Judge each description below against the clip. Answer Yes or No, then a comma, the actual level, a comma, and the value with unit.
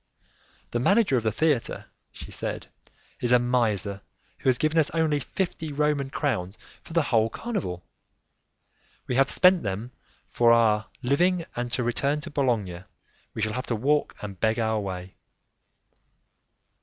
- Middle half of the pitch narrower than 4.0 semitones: No, wide, 5.4 semitones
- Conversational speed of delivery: Yes, average, 155 wpm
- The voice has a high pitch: No, low, 125 Hz